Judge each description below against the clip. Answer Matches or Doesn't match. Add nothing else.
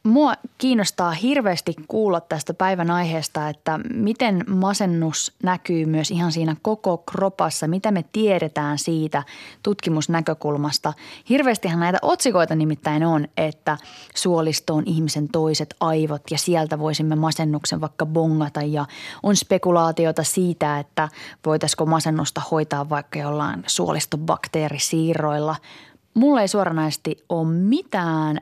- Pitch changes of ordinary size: Matches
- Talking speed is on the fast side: Doesn't match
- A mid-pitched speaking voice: Matches